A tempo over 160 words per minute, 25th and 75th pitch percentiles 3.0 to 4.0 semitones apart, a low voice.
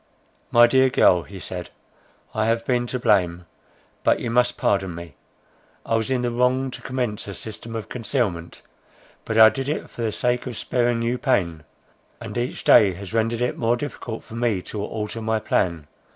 Yes: average, 190 wpm; average, 3.5 semitones; low, 115 Hz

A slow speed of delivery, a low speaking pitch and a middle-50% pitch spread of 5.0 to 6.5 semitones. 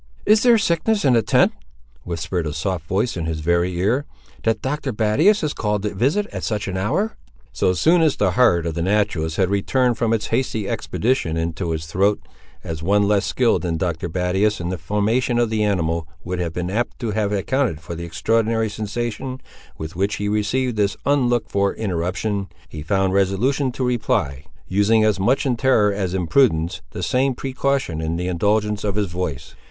No: average, 195 wpm; low, 105 Hz; wide, 5.4 semitones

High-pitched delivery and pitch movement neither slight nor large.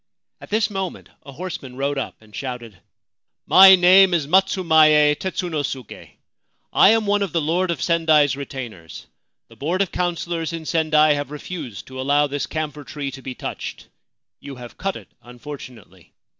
No: medium, 150 Hz; average, 4.6 semitones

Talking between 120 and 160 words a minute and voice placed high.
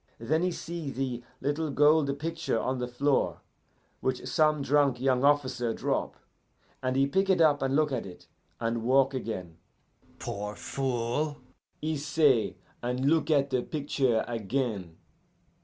No: average, 145 wpm; low, 135 Hz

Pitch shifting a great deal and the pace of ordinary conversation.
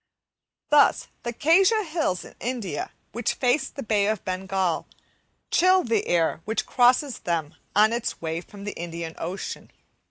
Yes: wide, 6.4 semitones; average, 150 wpm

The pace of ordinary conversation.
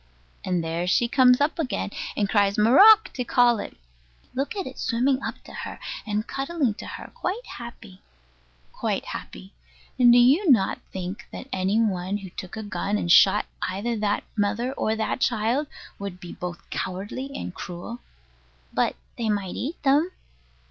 Yes: average, 170 wpm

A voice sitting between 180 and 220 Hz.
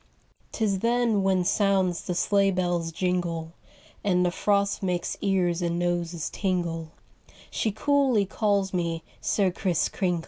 Yes: medium, 185 Hz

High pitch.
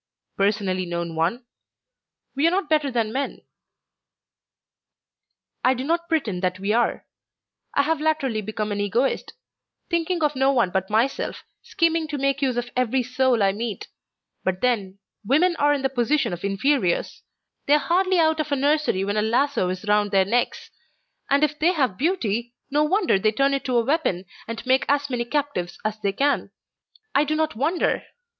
Yes: very high, 260 Hz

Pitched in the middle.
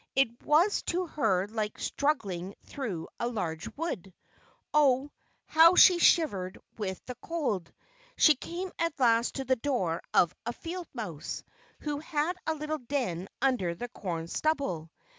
No: very high, 255 Hz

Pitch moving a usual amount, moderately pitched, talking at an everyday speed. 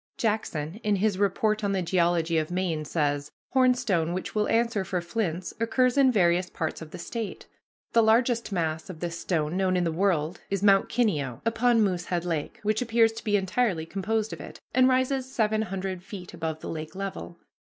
No: average, 4.8 semitones; high, 195 Hz; average, 190 wpm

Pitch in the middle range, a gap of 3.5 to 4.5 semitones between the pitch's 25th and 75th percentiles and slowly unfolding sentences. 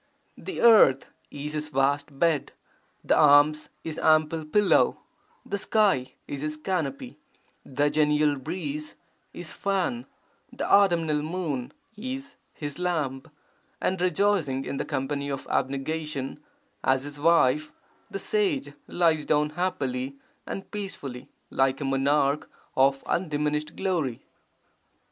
Yes: medium, 150 Hz; average, 4.1 semitones; slow, 120 wpm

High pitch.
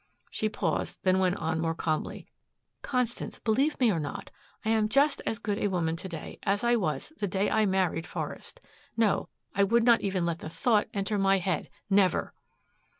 Yes: high, 200 Hz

